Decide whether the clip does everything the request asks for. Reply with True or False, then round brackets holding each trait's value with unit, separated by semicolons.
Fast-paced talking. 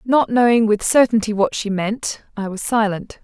False (185 wpm)